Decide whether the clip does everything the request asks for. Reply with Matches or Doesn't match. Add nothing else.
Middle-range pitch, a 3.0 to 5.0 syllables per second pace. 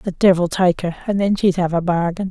Doesn't match